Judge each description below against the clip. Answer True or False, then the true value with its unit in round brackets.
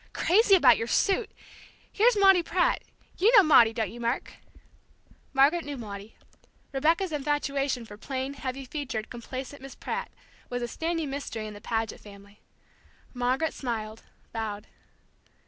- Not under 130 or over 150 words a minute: True (140 wpm)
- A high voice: True (270 Hz)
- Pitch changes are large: True (5.9 semitones)